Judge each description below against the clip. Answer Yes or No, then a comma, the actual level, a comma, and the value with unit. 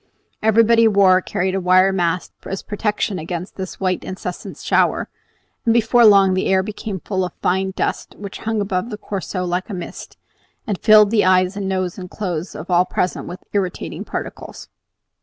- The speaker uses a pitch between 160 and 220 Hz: Yes, high, 190 Hz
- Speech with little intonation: Yes, narrow, 2.3 semitones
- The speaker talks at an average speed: Yes, average, 185 wpm